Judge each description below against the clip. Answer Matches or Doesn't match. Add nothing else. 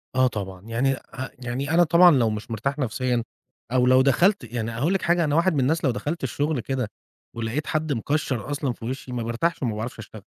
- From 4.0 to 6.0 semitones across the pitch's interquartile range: Matches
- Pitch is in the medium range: Doesn't match